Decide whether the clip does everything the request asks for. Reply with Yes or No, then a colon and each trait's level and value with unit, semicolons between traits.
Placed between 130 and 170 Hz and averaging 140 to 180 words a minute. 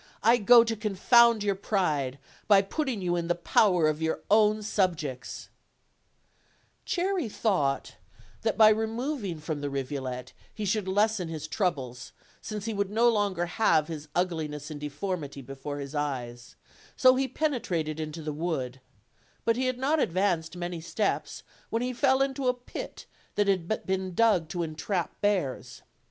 No: medium, 185 Hz; average, 160 wpm